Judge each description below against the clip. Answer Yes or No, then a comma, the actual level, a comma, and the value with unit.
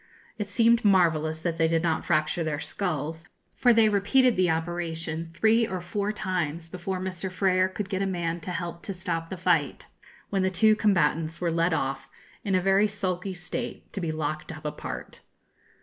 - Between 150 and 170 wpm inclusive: No, average, 185 wpm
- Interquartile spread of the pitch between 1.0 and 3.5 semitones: Yes, average, 3.1 semitones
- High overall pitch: No, medium, 175 Hz